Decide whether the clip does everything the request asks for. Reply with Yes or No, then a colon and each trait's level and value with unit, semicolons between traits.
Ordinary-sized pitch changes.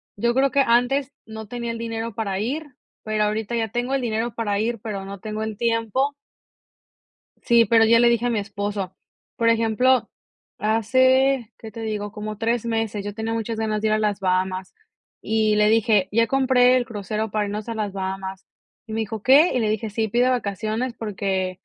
No: narrow, 2.2 semitones